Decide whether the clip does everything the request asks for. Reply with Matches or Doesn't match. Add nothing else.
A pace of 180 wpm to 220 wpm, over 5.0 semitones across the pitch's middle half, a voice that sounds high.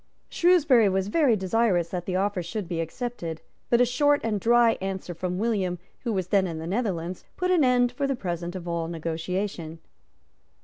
Matches